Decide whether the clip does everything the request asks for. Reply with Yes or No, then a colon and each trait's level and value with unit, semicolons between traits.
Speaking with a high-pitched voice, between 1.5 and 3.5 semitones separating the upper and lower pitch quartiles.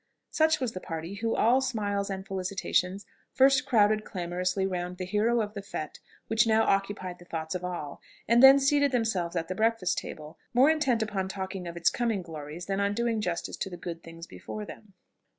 No: high, 195 Hz; average, 4.1 semitones